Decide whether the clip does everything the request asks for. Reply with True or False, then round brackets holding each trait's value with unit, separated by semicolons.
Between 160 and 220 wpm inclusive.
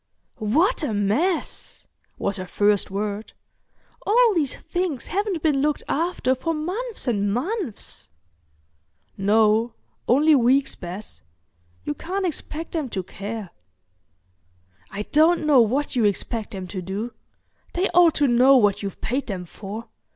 False (135 wpm)